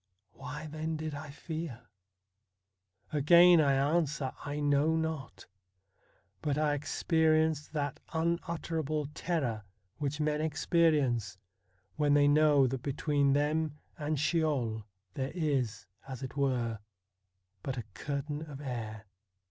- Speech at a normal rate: No, slow, 115 wpm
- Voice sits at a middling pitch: Yes, medium, 145 Hz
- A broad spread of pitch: No, average, 2.7 semitones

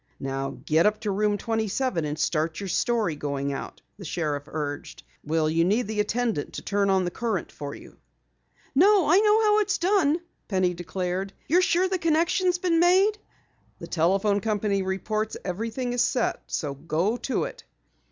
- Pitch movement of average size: No, wide, 8.7 semitones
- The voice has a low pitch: No, high, 205 Hz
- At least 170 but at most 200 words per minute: Yes, average, 175 wpm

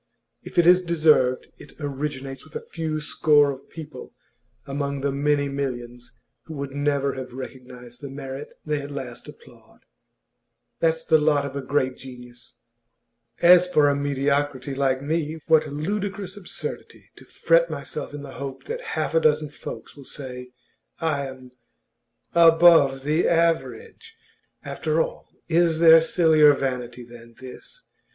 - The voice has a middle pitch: Yes, medium, 145 Hz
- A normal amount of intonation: Yes, average, 3.4 semitones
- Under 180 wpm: Yes, average, 145 wpm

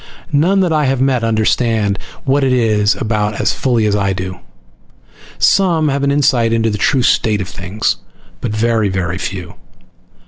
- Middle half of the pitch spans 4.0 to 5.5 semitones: Yes, average, 4.6 semitones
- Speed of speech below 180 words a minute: Yes, average, 170 wpm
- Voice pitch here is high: No, low, 115 Hz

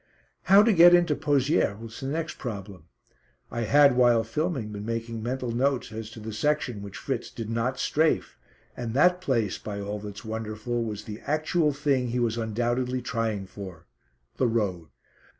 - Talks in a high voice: No, low, 120 Hz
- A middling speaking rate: Yes, average, 170 wpm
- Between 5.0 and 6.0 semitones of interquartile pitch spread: No, average, 4.5 semitones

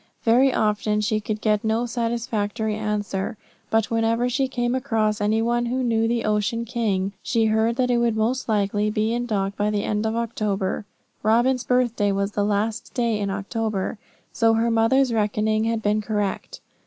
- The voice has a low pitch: No, high, 220 Hz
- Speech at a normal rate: Yes, average, 180 wpm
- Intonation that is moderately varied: No, narrow, 1.9 semitones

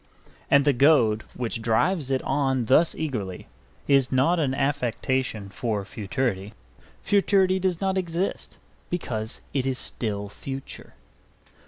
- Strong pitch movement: Yes, wide, 6.0 semitones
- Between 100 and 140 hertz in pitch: Yes, low, 135 Hz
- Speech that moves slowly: Yes, slow, 125 wpm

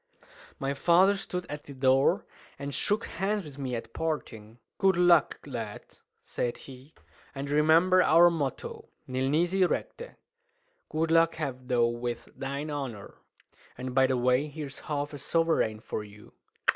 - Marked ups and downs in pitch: No, average, 4.5 semitones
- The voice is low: No, medium, 145 Hz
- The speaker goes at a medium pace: Yes, average, 150 wpm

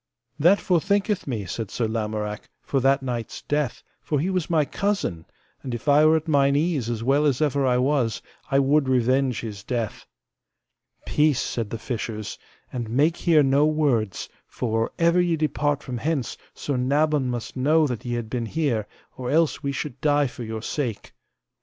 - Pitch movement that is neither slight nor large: Yes, average, 4.4 semitones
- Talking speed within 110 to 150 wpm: No, average, 185 wpm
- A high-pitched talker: No, low, 135 Hz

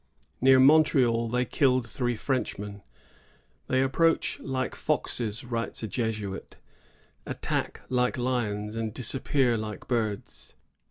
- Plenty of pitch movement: No, average, 3.0 semitones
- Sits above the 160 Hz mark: No, low, 120 Hz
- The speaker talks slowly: Yes, slow, 110 wpm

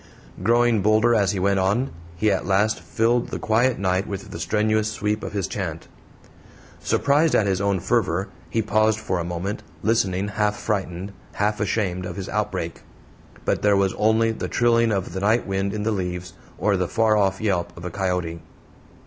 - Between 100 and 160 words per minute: No, average, 185 wpm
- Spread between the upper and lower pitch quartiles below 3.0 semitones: Yes, narrow, 2.4 semitones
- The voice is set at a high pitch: No, low, 100 Hz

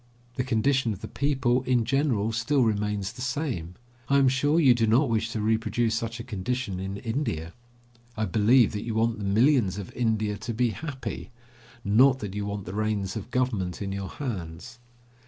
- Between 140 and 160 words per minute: No, average, 190 wpm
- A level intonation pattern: No, average, 3.7 semitones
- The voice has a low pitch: Yes, low, 115 Hz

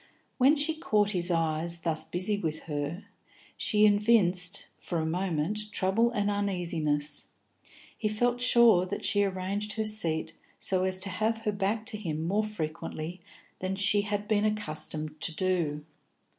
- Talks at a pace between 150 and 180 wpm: Yes, average, 155 wpm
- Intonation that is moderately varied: Yes, average, 4.2 semitones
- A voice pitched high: Yes, high, 195 Hz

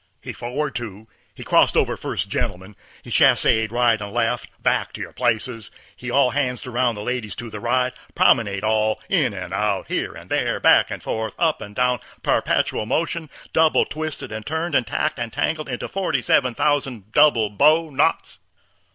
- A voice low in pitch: Yes, low, 120 Hz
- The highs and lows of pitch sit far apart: No, average, 4.7 semitones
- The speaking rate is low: No, average, 175 wpm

